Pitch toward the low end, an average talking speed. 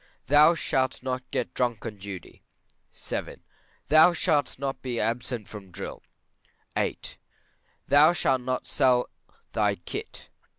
No: low, 130 Hz; slow, 125 wpm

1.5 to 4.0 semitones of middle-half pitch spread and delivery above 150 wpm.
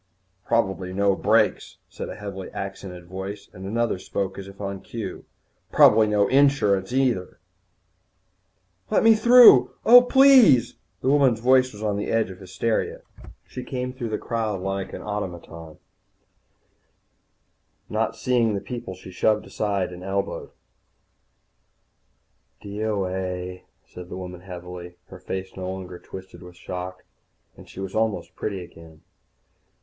No: average, 3.6 semitones; average, 140 wpm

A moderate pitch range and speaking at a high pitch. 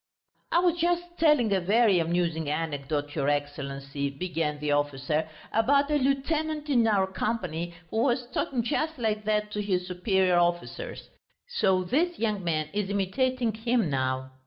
No: wide, 7.9 semitones; high, 195 Hz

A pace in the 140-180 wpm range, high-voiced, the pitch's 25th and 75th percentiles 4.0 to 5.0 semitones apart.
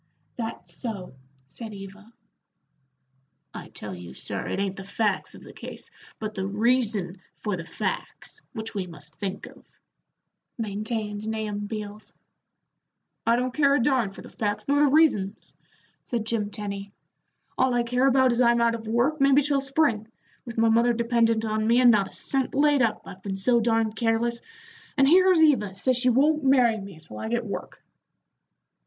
No: average, 175 wpm; high, 225 Hz; average, 3.6 semitones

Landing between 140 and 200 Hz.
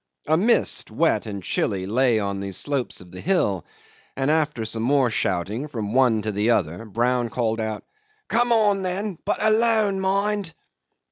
No: low, 125 Hz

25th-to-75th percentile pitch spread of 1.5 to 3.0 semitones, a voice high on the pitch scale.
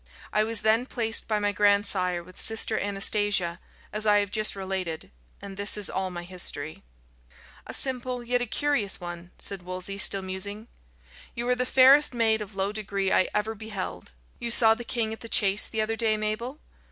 Yes: average, 2.7 semitones; high, 210 Hz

